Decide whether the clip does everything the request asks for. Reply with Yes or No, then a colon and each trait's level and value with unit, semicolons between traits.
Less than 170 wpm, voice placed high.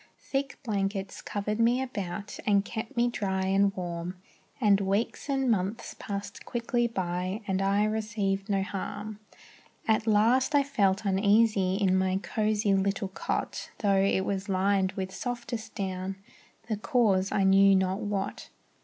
Yes: average, 145 wpm; high, 200 Hz